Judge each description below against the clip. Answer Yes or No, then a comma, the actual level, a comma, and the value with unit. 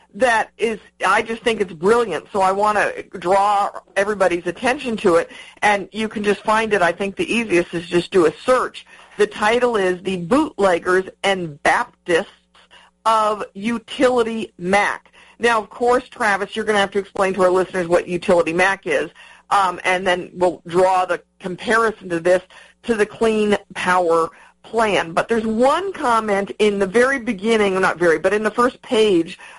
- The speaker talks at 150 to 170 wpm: No, average, 180 wpm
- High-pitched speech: Yes, high, 200 Hz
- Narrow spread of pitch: No, average, 3.6 semitones